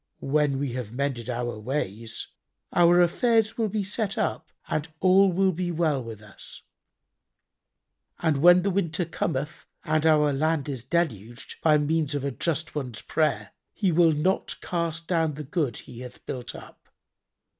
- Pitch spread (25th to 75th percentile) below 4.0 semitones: No, average, 4.9 semitones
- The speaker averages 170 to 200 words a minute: No, average, 160 wpm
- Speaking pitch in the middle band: Yes, medium, 155 Hz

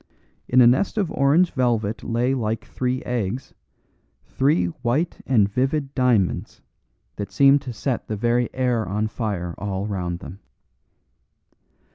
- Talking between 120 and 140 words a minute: Yes, slow, 135 wpm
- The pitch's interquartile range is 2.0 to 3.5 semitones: No, average, 4.2 semitones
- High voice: No, low, 120 Hz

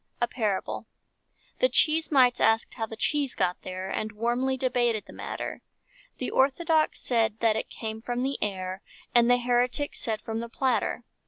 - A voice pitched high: Yes, high, 240 Hz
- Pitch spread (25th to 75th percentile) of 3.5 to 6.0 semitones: No, average, 3.0 semitones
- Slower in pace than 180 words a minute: Yes, average, 170 wpm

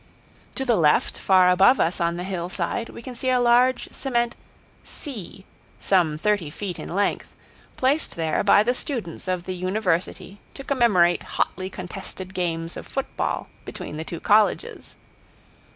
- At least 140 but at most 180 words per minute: Yes, average, 150 wpm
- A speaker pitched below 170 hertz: No, high, 190 Hz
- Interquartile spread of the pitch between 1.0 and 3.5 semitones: No, wide, 5.4 semitones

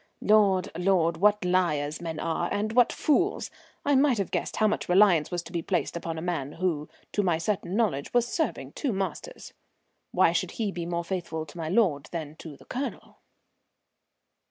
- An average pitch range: Yes, average, 4.4 semitones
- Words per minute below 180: No, average, 185 wpm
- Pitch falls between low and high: Yes, medium, 180 Hz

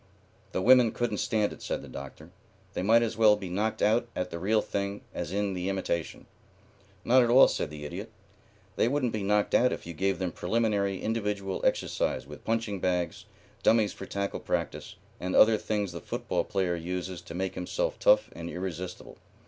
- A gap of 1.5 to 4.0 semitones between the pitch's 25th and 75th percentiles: Yes, average, 3.6 semitones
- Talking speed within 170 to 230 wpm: Yes, average, 190 wpm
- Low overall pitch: Yes, low, 100 Hz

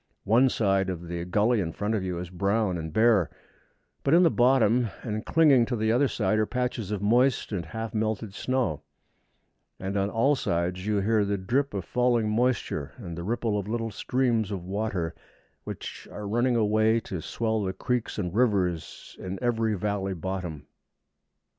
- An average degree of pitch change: Yes, average, 3.9 semitones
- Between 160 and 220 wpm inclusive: Yes, average, 180 wpm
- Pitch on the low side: Yes, low, 105 Hz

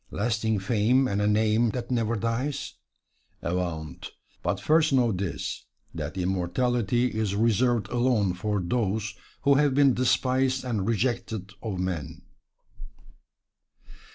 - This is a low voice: Yes, low, 110 Hz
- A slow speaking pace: Yes, slow, 120 wpm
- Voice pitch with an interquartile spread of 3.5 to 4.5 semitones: Yes, average, 4.1 semitones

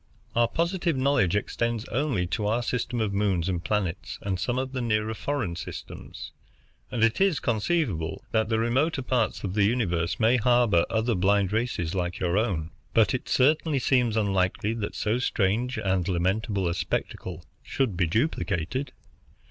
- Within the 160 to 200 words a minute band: Yes, average, 165 wpm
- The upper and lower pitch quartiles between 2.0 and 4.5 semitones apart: No, average, 4.9 semitones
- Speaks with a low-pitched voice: Yes, low, 110 Hz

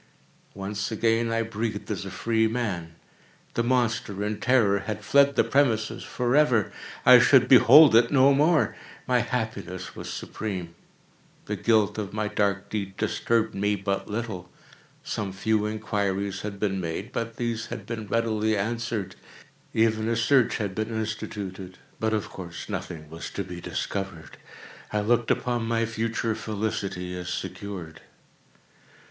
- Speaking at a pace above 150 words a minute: No, average, 140 wpm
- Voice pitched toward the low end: Yes, low, 110 Hz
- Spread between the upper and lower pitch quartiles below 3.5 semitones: Yes, average, 2.7 semitones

